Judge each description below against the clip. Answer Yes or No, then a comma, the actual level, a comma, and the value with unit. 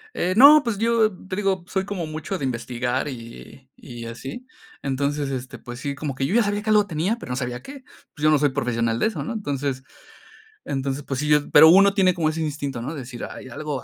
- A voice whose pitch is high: No, medium, 150 Hz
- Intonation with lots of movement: Yes, wide, 6.8 semitones